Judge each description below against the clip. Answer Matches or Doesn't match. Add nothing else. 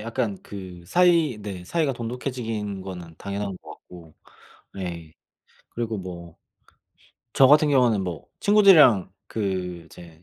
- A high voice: Doesn't match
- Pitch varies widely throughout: Matches